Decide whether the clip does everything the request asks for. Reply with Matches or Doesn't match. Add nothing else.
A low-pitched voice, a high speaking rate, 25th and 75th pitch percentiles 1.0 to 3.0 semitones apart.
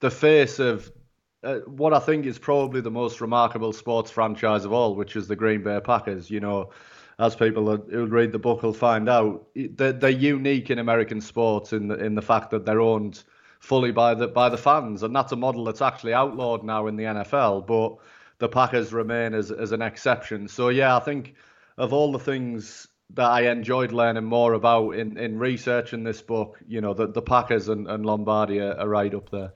Matches